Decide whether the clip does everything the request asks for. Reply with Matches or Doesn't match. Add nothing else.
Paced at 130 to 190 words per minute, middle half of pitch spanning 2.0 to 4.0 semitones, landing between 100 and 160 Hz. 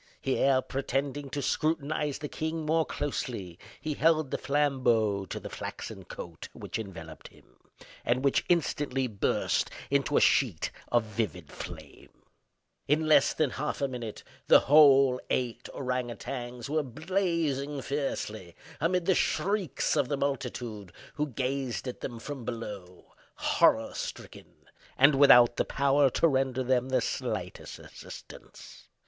Matches